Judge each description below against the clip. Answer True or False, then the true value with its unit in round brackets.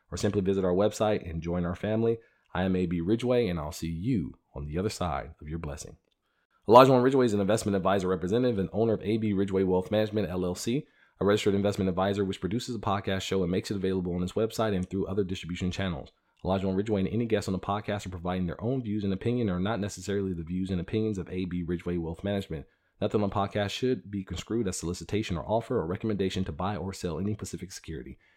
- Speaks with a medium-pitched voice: False (95 Hz)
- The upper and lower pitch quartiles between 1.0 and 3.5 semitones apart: True (2.8 semitones)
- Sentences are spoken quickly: True (225 wpm)